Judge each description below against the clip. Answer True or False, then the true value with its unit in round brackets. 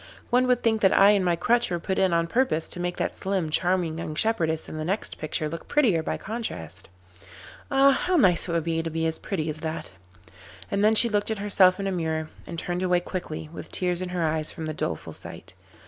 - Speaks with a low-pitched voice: False (175 Hz)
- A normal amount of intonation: True (4.0 semitones)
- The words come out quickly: True (235 wpm)